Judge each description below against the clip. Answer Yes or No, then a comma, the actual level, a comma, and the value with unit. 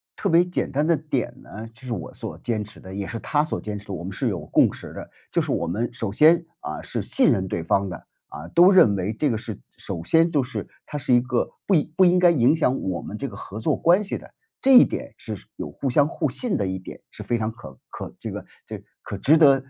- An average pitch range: No, wide, 7.7 semitones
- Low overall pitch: Yes, low, 120 Hz